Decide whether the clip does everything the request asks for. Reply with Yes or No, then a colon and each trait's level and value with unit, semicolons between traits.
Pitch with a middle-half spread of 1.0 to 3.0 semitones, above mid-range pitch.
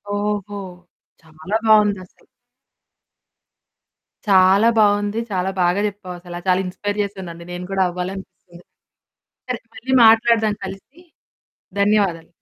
Yes: narrow, 2.4 semitones; high, 195 Hz